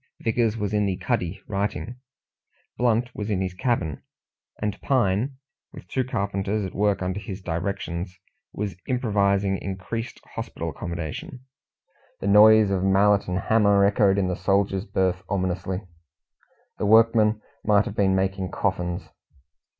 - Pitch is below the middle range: Yes, low, 100 Hz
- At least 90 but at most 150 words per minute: Yes, slow, 135 wpm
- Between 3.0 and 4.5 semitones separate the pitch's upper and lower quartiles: No, narrow, 2.4 semitones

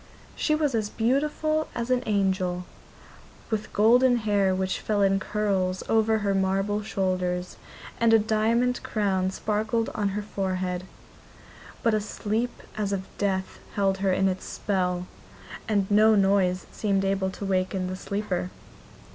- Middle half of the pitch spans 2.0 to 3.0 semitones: Yes, narrow, 2.5 semitones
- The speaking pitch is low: No, high, 200 Hz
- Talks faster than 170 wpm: No, average, 145 wpm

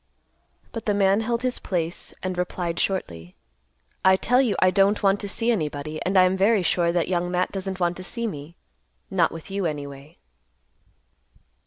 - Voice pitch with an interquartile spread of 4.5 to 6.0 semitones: No, average, 2.9 semitones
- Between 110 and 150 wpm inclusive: No, average, 180 wpm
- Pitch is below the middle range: No, medium, 185 Hz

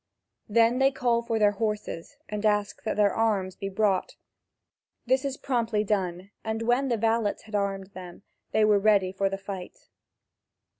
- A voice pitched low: No, high, 210 Hz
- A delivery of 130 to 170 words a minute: Yes, average, 165 wpm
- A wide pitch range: No, narrow, 2.6 semitones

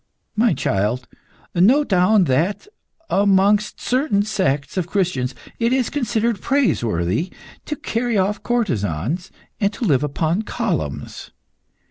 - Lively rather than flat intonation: Yes, wide, 8.3 semitones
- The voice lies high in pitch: Yes, high, 195 Hz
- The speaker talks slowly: Yes, slow, 110 wpm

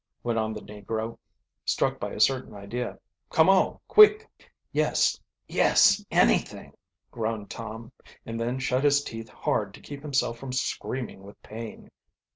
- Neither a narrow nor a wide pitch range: Yes, average, 3.6 semitones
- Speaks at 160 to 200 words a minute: No, average, 145 wpm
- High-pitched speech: No, low, 115 Hz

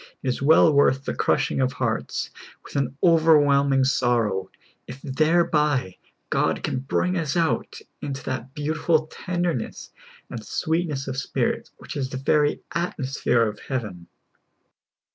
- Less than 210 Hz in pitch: Yes, medium, 140 Hz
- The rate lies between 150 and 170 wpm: No, average, 140 wpm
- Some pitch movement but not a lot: Yes, average, 3.3 semitones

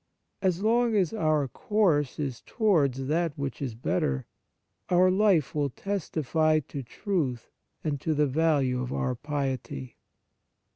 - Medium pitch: Yes, medium, 150 Hz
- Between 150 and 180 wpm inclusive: No, slow, 135 wpm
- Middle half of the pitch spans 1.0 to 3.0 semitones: No, wide, 5.4 semitones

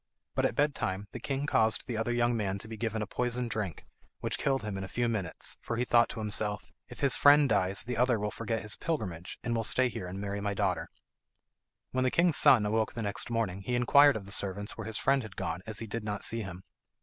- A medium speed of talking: No, fast, 250 wpm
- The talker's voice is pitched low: Yes, low, 110 Hz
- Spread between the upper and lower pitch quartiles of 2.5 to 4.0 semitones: Yes, average, 3.2 semitones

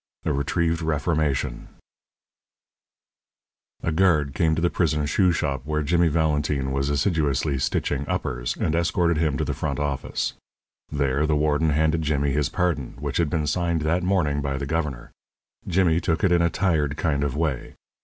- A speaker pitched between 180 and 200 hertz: No, very low, 75 Hz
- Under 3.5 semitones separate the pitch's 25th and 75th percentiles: Yes, average, 2.7 semitones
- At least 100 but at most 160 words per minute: No, average, 170 wpm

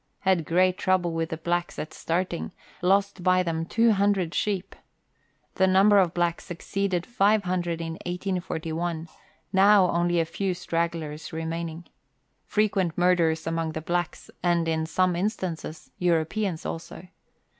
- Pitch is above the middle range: No, medium, 175 Hz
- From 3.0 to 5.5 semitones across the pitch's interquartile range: No, narrow, 2.4 semitones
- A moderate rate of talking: No, slow, 130 wpm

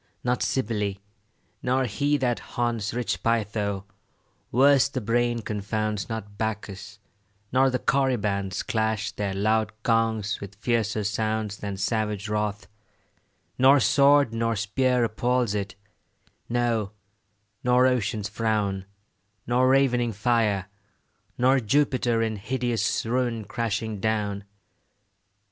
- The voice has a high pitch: No, low, 110 Hz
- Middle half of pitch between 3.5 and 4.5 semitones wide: No, average, 2.9 semitones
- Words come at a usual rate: No, slow, 110 wpm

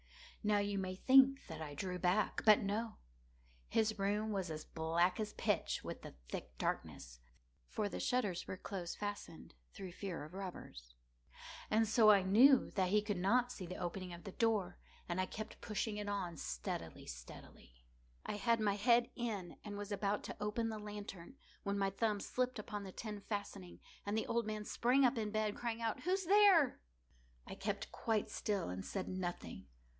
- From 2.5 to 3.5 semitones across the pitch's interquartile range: Yes, average, 3.1 semitones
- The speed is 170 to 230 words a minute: Yes, average, 180 wpm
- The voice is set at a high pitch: Yes, high, 205 Hz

